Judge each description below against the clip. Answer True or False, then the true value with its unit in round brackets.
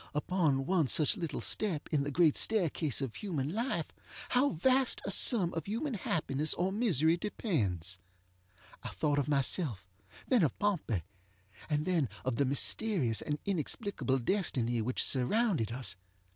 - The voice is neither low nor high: True (160 Hz)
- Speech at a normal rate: True (145 wpm)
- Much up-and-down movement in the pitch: True (6.9 semitones)